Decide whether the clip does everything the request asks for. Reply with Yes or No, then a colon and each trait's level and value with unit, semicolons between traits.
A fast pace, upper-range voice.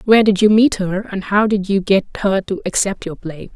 Yes: fast, 255 wpm; high, 200 Hz